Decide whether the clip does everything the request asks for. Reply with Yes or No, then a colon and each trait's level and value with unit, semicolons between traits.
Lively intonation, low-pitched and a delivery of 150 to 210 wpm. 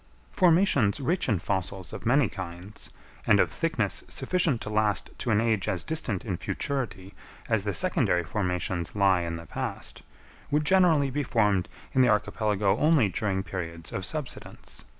Yes: wide, 6.6 semitones; low, 105 Hz; average, 160 wpm